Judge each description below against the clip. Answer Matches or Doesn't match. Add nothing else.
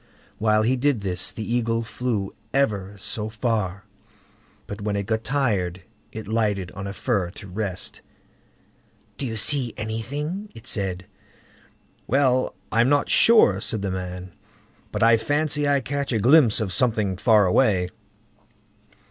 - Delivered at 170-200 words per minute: Doesn't match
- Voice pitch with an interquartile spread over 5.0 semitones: Doesn't match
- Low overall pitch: Matches